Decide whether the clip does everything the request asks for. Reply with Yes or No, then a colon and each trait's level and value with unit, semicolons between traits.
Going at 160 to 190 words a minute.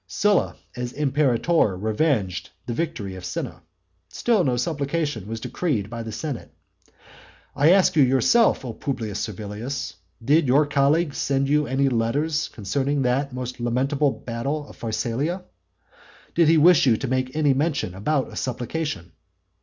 No: average, 145 wpm